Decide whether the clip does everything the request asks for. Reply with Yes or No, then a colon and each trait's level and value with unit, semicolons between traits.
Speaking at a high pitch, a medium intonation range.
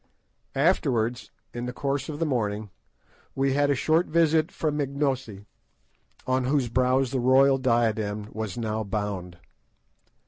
No: low, 130 Hz; average, 4.3 semitones